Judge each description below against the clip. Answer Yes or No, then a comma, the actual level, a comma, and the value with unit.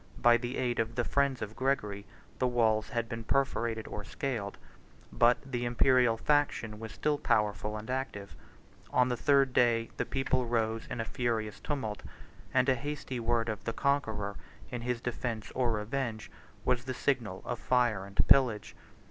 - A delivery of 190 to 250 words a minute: No, average, 170 wpm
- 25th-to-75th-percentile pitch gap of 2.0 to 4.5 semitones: Yes, average, 2.7 semitones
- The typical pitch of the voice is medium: No, low, 120 Hz